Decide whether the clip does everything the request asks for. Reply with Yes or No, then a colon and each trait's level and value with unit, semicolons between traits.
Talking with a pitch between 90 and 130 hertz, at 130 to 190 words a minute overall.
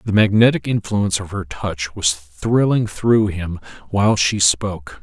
Yes: low, 100 Hz; average, 155 wpm